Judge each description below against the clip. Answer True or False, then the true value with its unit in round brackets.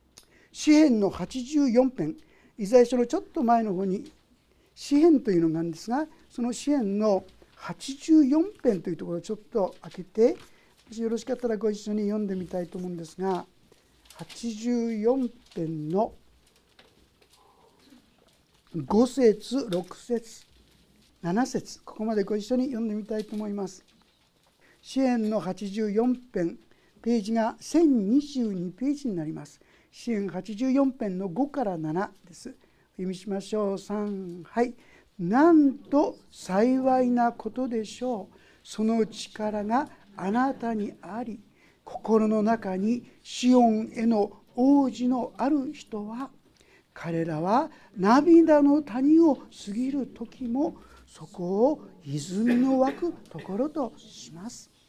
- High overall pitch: True (225 Hz)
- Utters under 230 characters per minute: True (220 characters per minute)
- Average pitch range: True (4.5 semitones)